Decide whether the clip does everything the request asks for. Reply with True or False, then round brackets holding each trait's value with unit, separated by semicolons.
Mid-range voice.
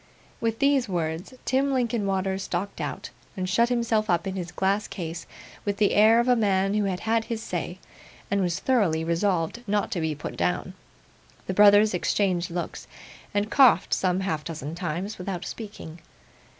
False (195 Hz)